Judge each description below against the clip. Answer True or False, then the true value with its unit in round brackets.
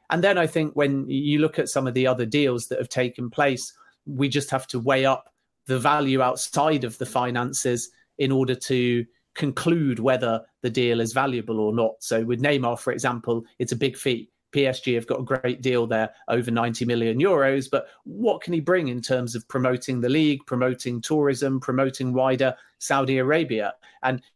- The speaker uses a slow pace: False (190 wpm)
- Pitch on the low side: True (130 Hz)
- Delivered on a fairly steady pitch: True (2.2 semitones)